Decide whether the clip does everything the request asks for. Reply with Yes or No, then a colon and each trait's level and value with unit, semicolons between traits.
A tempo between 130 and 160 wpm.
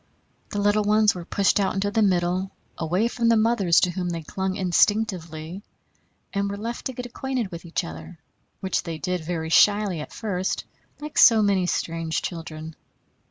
No: average, 175 wpm